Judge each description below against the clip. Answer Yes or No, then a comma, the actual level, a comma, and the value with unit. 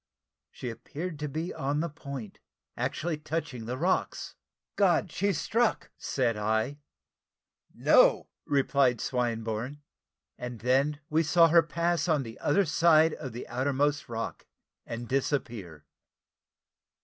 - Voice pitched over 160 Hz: No, medium, 140 Hz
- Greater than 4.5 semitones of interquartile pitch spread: Yes, average, 4.9 semitones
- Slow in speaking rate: Yes, slow, 125 wpm